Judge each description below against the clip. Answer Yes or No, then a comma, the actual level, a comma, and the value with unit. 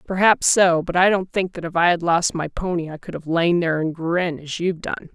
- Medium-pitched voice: Yes, medium, 170 Hz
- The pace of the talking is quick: Yes, fast, 270 wpm